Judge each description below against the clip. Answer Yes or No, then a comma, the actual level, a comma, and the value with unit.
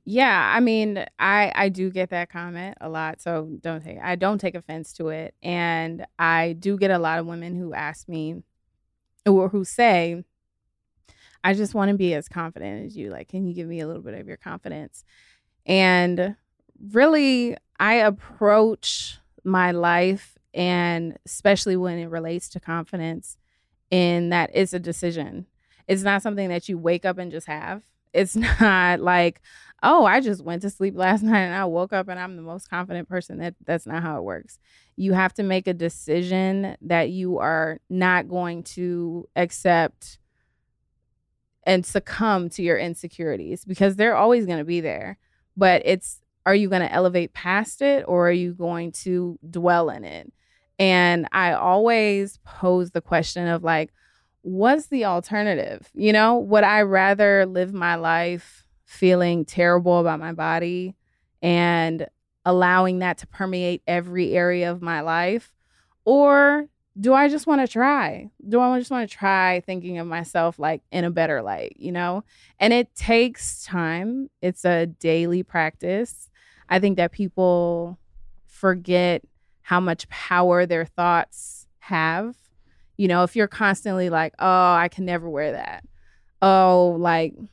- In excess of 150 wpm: Yes, average, 165 wpm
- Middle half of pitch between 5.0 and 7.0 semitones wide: No, narrow, 2.6 semitones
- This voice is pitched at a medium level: Yes, medium, 180 Hz